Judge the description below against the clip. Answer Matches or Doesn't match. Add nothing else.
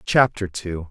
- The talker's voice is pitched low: Matches